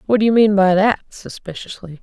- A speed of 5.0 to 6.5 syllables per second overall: Yes, 5.6 syllables/s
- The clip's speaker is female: Yes, female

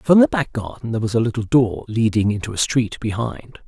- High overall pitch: No, low, 115 Hz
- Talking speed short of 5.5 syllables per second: No, 5.7 syllables/s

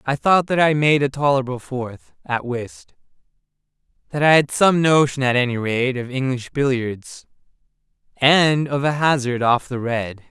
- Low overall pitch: Yes, low, 130 Hz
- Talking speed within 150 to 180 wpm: Yes, average, 165 wpm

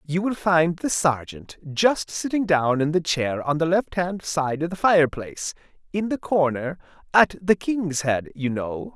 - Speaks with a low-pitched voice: No, medium, 160 Hz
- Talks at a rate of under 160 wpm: No, average, 180 wpm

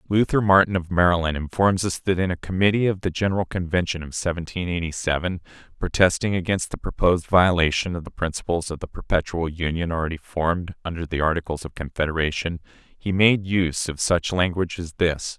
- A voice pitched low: Yes, very low, 85 Hz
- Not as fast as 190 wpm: Yes, average, 175 wpm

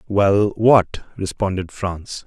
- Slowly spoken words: Yes, slow, 80 wpm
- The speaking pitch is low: Yes, low, 100 Hz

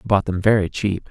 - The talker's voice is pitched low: Yes, low, 100 Hz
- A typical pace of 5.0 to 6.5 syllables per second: Yes, 5.9 syllables/s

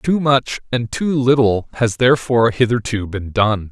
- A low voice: Yes, low, 120 Hz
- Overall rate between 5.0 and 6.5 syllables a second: No, 4.6 syllables/s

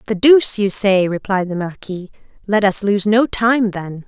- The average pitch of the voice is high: Yes, high, 200 Hz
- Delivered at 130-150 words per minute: No, average, 190 wpm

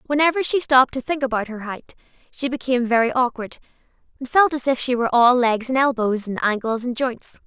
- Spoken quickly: Yes, fast, 210 wpm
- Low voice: No, very high, 250 Hz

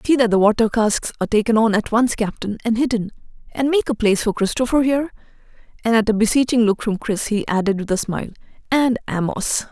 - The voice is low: No, high, 225 Hz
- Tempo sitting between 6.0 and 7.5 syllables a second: Yes, 6.2 syllables/s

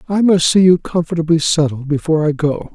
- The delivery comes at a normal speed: Yes, average, 195 wpm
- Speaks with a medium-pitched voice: Yes, medium, 160 Hz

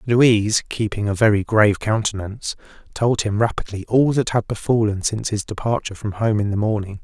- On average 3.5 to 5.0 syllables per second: No, 5.8 syllables/s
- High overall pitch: No, low, 105 Hz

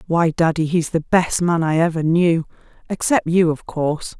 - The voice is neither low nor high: Yes, medium, 165 Hz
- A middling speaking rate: Yes, average, 170 wpm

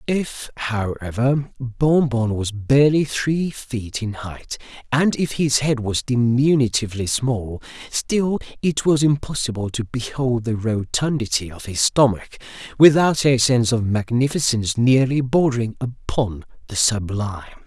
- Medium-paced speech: No, slow, 130 wpm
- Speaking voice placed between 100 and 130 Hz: Yes, low, 125 Hz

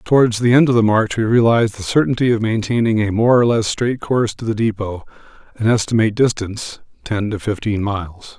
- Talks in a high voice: No, low, 110 Hz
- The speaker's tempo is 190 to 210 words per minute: Yes, average, 200 wpm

